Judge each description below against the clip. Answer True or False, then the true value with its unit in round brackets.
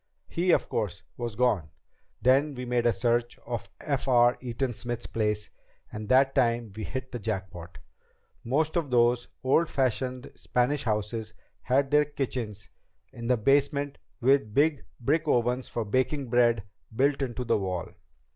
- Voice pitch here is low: True (125 Hz)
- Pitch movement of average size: True (3.1 semitones)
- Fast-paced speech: False (155 wpm)